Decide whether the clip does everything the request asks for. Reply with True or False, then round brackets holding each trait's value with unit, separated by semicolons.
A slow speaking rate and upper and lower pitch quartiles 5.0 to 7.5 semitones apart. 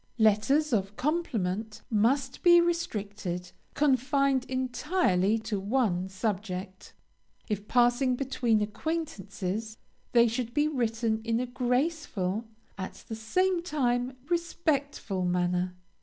True (105 wpm; 5.3 semitones)